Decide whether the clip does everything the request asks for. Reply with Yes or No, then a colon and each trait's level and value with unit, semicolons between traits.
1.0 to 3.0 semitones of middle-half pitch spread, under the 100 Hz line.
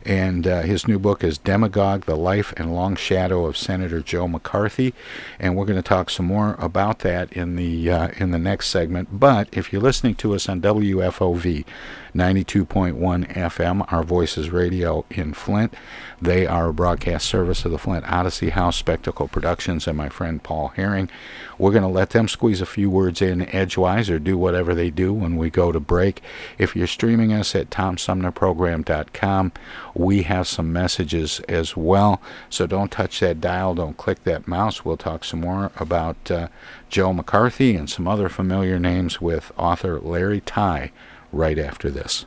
Yes: narrow, 2.4 semitones; very low, 90 Hz